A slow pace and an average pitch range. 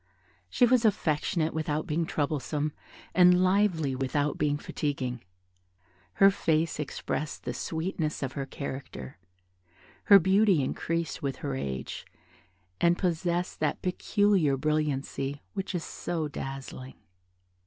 Yes: slow, 115 wpm; average, 4.3 semitones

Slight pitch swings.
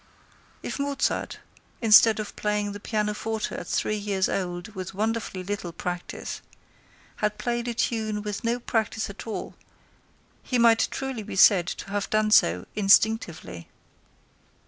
Yes: narrow, 2.3 semitones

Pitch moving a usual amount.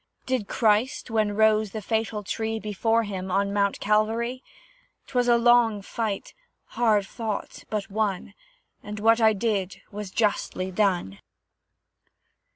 No: narrow, 2.1 semitones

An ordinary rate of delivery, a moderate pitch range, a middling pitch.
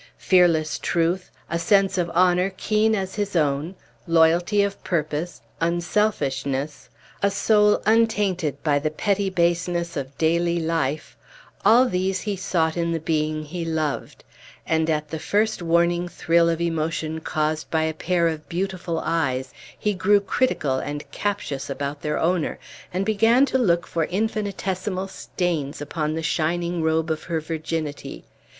Yes: average, 145 wpm; average, 3.4 semitones; medium, 170 Hz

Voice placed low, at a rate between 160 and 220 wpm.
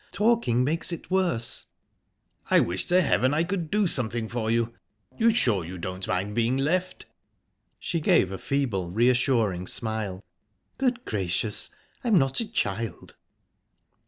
No: low, 120 Hz; slow, 135 wpm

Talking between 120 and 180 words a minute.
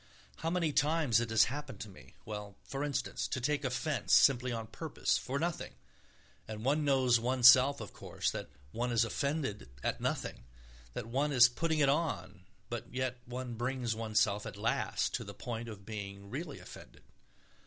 Yes: average, 170 wpm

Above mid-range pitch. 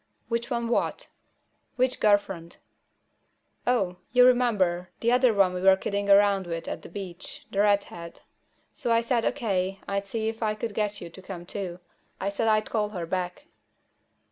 Yes: high, 200 Hz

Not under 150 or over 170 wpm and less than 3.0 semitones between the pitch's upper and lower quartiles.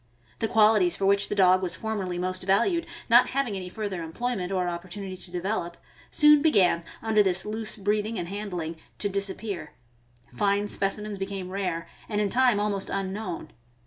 Yes: average, 165 wpm; narrow, 2.6 semitones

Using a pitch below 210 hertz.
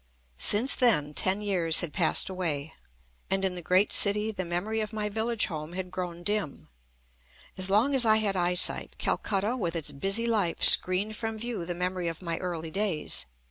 Yes: high, 190 Hz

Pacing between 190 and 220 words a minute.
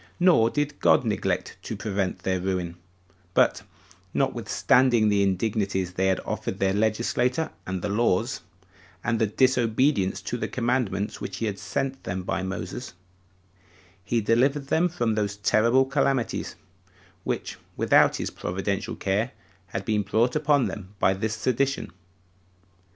No: slow, 135 wpm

